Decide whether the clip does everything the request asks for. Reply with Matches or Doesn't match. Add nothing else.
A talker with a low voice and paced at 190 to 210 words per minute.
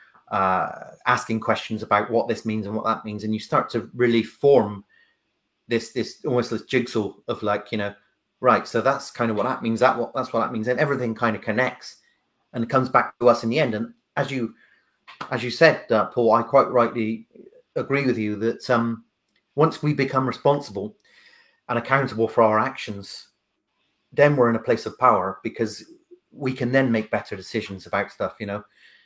Matches